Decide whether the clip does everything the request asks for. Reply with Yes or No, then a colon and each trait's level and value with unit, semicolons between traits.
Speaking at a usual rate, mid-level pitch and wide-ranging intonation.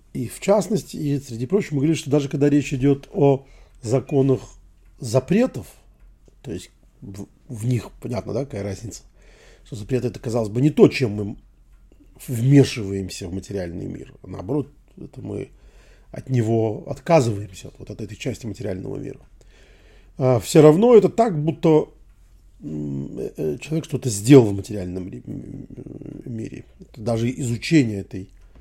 No: average, 140 wpm; low, 125 Hz; wide, 5.8 semitones